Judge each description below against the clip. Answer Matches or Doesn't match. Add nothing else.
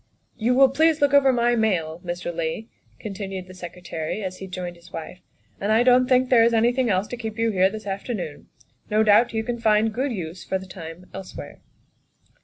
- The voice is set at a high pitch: Matches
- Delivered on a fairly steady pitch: Doesn't match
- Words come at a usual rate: Doesn't match